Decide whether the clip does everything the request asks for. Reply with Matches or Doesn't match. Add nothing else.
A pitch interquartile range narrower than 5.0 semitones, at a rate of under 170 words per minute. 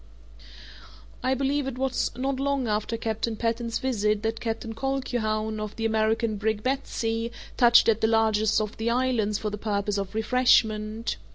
Matches